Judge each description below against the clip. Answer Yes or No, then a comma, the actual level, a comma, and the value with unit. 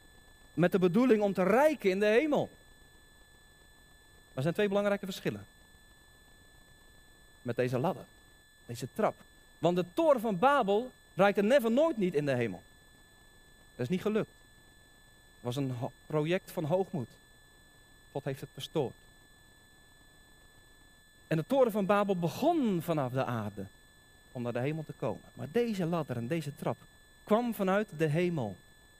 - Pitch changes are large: Yes, wide, 8.6 semitones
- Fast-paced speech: No, average, 150 wpm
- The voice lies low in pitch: No, medium, 160 Hz